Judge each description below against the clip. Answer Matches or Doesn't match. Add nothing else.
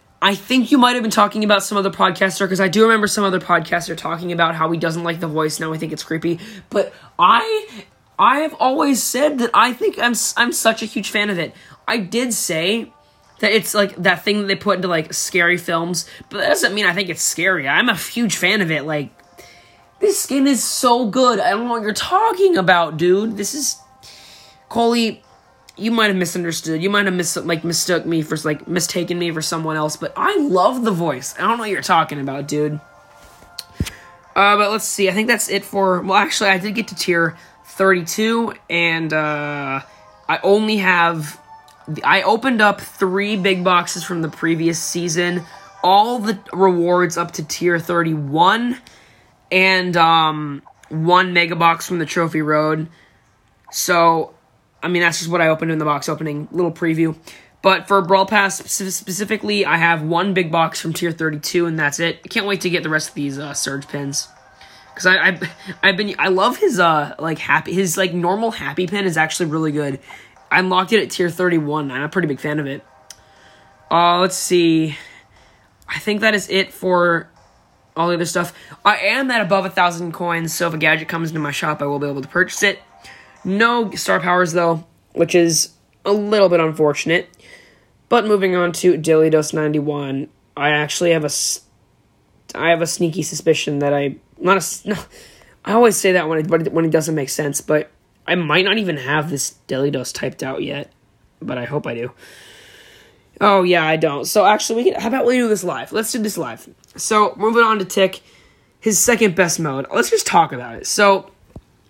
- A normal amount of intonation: Matches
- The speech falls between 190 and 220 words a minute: Matches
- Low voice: Doesn't match